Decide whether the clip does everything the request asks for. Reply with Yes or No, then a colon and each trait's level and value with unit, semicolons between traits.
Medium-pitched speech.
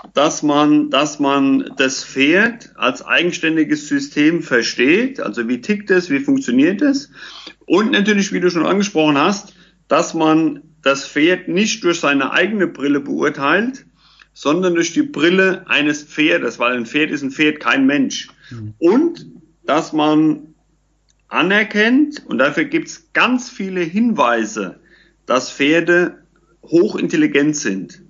Yes: medium, 170 Hz